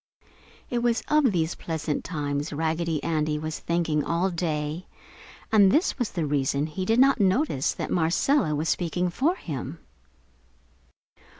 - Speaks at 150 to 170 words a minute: No, average, 140 wpm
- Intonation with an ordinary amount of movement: Yes, average, 4.6 semitones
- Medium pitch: Yes, medium, 165 Hz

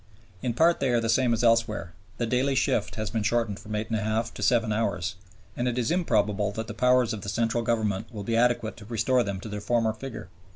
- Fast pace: Yes, fast, 235 wpm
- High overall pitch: No, low, 115 Hz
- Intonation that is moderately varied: No, narrow, 2.1 semitones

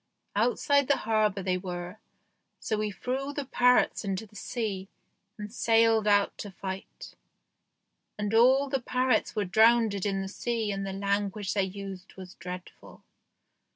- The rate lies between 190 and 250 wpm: No, average, 150 wpm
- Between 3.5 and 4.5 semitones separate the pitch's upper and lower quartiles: No, average, 3.0 semitones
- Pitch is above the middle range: Yes, high, 210 Hz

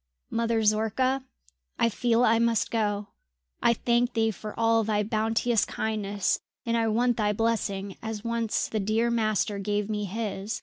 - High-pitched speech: Yes, high, 220 Hz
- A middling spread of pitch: No, narrow, 1.7 semitones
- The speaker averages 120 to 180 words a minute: Yes, average, 160 wpm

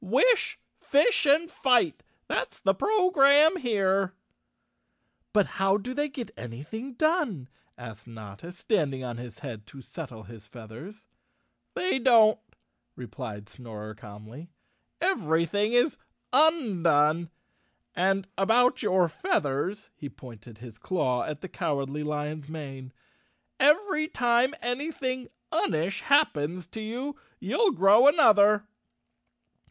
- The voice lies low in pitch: No, high, 190 Hz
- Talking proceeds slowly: Yes, slow, 115 wpm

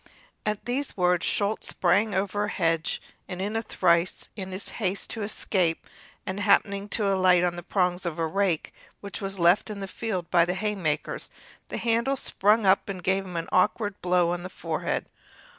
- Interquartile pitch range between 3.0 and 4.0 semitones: No, narrow, 2.5 semitones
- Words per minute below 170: No, average, 185 wpm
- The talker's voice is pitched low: No, high, 190 Hz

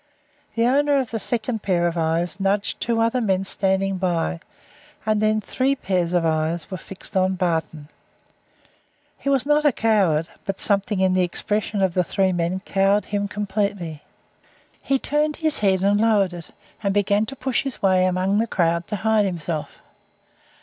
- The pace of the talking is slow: No, average, 175 wpm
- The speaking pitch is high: Yes, high, 195 Hz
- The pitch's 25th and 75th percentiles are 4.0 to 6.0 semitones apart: No, average, 3.6 semitones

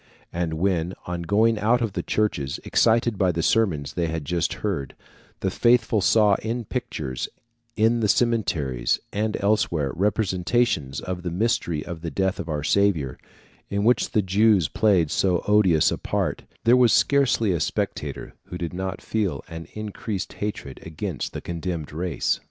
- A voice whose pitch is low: Yes, very low, 95 Hz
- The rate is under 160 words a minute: No, average, 165 wpm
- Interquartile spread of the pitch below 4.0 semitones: No, average, 4.7 semitones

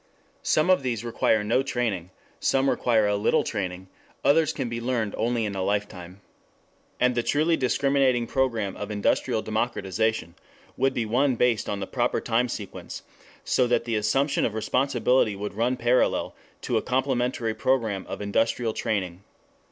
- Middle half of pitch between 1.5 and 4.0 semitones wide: Yes, average, 3.5 semitones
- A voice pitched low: Yes, low, 115 Hz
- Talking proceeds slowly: No, average, 160 wpm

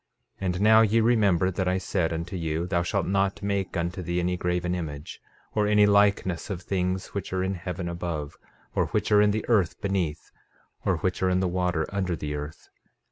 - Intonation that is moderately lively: No, narrow, 2.3 semitones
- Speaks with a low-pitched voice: Yes, very low, 90 Hz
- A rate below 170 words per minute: No, fast, 205 wpm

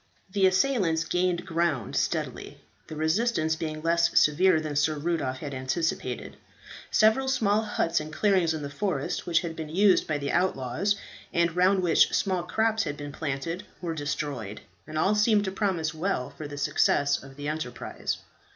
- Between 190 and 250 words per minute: No, average, 170 wpm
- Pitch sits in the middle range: Yes, medium, 165 Hz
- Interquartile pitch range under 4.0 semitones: No, average, 4.3 semitones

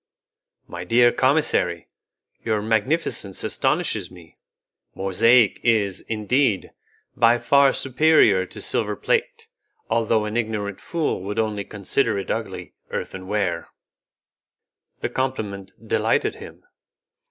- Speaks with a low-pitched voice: Yes, low, 110 Hz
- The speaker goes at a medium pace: No, slow, 105 wpm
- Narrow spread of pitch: No, average, 4.6 semitones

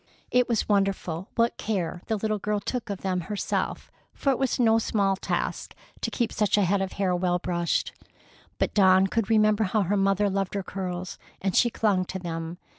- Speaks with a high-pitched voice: Yes, high, 195 Hz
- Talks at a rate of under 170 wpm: No, average, 195 wpm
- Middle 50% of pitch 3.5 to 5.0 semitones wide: No, narrow, 2.6 semitones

